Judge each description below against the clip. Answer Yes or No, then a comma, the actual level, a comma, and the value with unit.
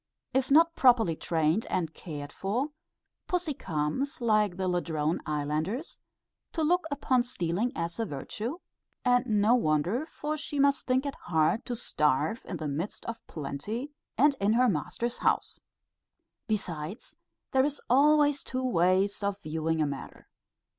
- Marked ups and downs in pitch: Yes, wide, 8.3 semitones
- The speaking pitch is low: No, high, 215 Hz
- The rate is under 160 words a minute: Yes, average, 145 wpm